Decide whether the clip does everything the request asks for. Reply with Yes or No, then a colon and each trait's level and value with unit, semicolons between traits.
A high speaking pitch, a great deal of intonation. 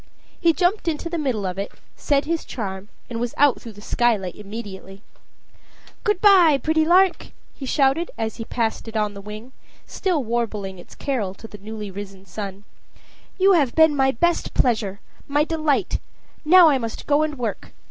Yes: high, 240 Hz; wide, 7.0 semitones